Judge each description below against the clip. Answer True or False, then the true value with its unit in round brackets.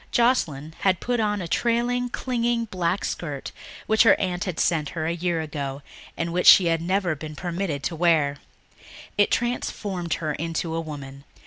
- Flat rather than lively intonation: False (4.7 semitones)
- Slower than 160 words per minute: False (175 wpm)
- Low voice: False (170 Hz)